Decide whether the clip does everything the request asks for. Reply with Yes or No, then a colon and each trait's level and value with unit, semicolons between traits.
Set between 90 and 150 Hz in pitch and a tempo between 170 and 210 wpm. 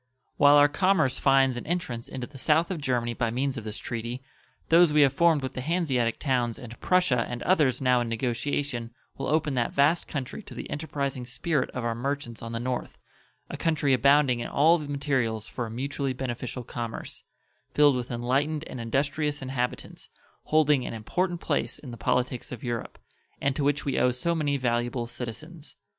Yes: low, 135 Hz; average, 190 wpm